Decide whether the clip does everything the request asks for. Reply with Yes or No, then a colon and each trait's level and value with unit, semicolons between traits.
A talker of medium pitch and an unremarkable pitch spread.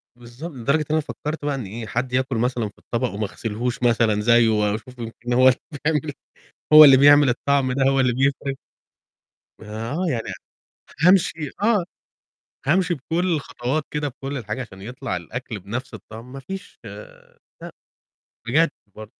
No: low, 130 Hz; average, 4.2 semitones